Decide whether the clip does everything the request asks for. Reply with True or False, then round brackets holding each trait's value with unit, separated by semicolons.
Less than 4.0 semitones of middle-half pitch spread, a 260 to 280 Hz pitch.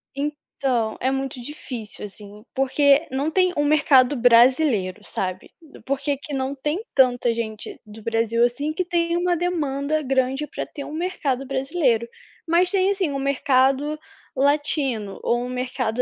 True (3.6 semitones; 270 Hz)